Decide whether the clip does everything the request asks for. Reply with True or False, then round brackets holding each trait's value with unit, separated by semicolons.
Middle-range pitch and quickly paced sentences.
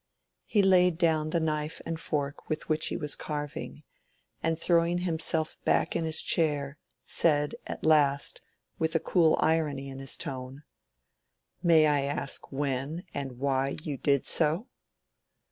False (155 Hz; 145 wpm)